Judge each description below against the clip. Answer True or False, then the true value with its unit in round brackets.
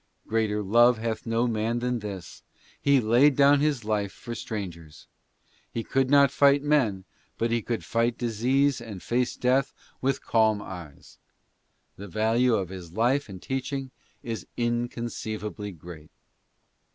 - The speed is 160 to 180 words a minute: False (150 wpm)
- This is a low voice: True (115 Hz)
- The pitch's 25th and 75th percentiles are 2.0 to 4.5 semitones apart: True (3.5 semitones)